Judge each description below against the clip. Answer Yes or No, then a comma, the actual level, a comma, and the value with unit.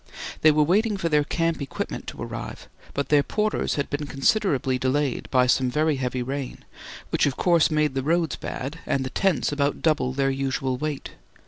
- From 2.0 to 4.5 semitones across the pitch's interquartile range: Yes, average, 2.9 semitones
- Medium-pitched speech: Yes, medium, 145 Hz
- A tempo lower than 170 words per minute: No, average, 190 wpm